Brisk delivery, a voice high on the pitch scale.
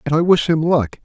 No: fast, 290 wpm; medium, 155 Hz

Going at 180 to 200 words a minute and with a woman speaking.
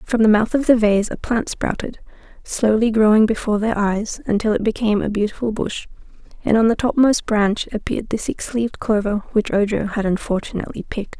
Yes: average, 190 wpm; female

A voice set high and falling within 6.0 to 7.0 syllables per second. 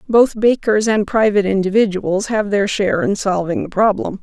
No: high, 205 Hz; 5.2 syllables/s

